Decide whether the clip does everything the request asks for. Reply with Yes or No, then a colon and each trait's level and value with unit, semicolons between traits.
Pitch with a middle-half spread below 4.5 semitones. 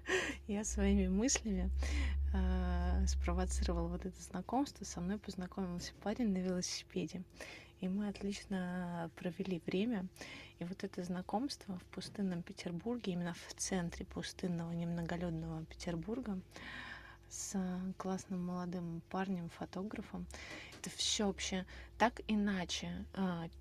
Yes: narrow, 2.6 semitones